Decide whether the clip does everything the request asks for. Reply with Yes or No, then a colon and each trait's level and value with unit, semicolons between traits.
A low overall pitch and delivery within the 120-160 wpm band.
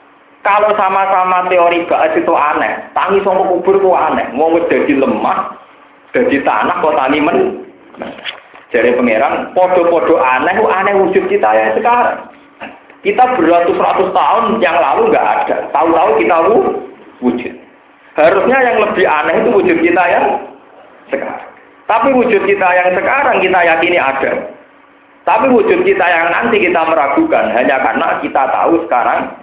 No: high, 195 Hz; average, 135 wpm